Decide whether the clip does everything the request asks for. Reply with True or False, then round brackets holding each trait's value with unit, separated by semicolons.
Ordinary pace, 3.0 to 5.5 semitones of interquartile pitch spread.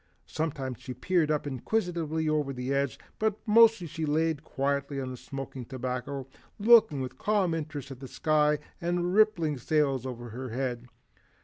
True (165 wpm; 4.1 semitones)